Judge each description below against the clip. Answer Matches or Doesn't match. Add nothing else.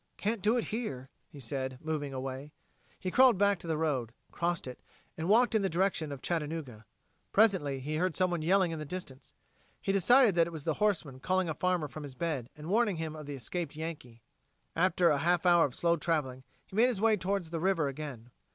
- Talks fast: Matches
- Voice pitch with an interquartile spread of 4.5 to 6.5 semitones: Matches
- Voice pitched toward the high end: Doesn't match